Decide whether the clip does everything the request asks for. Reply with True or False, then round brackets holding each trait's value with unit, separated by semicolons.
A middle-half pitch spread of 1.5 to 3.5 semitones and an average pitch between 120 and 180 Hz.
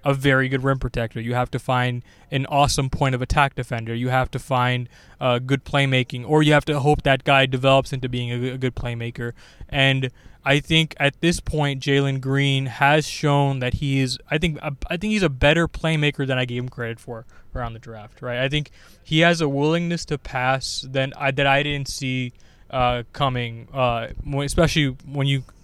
True (2.4 semitones; 135 Hz)